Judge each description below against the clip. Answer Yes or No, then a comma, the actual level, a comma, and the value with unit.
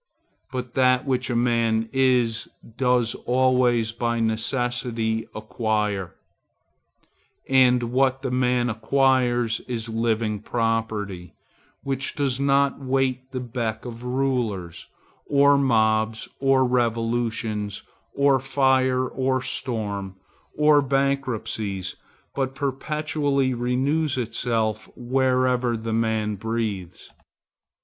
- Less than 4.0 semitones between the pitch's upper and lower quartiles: Yes, average, 2.9 semitones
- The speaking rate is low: Yes, slow, 95 wpm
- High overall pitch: No, low, 125 Hz